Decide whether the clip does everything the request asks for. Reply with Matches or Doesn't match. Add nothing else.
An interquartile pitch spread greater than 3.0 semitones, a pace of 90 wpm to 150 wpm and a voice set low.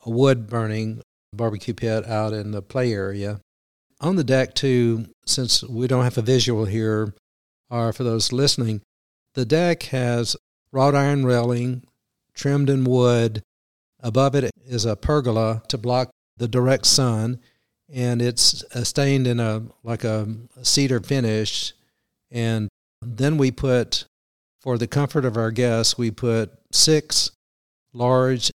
Doesn't match